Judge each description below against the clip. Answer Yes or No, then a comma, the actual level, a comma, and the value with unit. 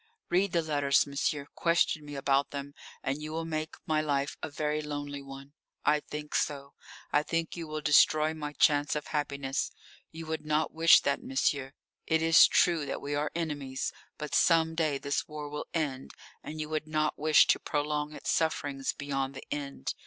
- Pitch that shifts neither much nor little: No, narrow, 1.8 semitones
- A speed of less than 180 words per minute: No, average, 185 wpm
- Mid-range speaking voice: Yes, medium, 150 Hz